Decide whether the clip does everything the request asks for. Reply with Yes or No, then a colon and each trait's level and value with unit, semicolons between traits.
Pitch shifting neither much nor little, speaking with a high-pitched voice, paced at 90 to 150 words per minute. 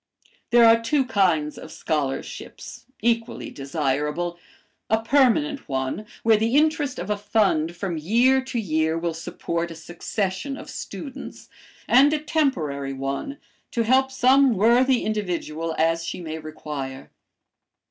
No: wide, 8.1 semitones; high, 200 Hz; slow, 135 wpm